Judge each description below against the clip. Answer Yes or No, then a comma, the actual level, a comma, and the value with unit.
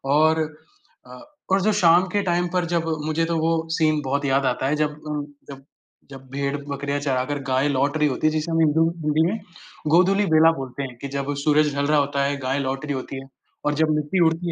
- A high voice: No, medium, 150 Hz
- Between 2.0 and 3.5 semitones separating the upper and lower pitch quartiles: Yes, average, 2.8 semitones